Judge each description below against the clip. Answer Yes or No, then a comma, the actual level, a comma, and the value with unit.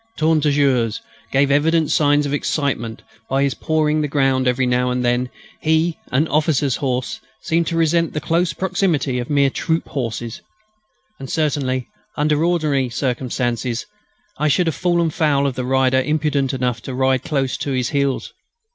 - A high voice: No, medium, 140 Hz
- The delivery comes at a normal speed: Yes, average, 165 wpm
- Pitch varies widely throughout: No, average, 3.2 semitones